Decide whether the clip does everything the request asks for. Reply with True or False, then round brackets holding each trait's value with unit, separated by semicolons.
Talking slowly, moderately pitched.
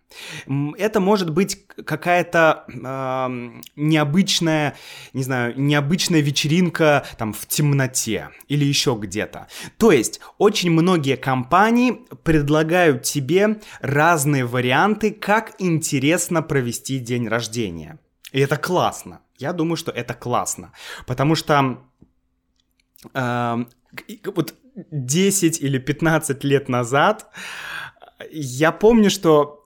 True (100 wpm; 145 Hz)